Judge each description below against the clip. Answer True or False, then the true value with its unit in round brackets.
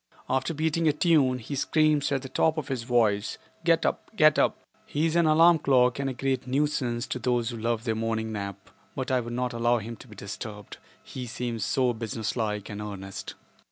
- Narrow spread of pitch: False (3.8 semitones)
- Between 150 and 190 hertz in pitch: False (125 Hz)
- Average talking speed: False (210 wpm)